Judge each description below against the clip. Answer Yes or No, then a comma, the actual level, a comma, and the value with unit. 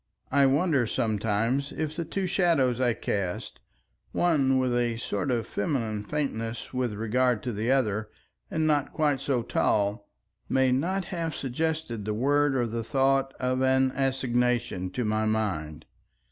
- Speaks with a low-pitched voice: Yes, low, 130 Hz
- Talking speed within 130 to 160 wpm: Yes, average, 150 wpm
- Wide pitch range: No, average, 4.0 semitones